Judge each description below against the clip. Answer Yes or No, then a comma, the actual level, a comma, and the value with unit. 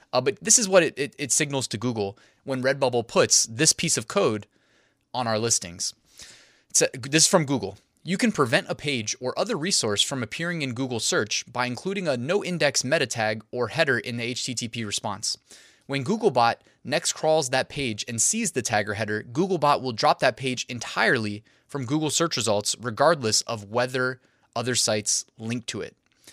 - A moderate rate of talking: Yes, average, 185 wpm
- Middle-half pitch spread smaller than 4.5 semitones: No, average, 4.9 semitones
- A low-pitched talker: Yes, low, 130 Hz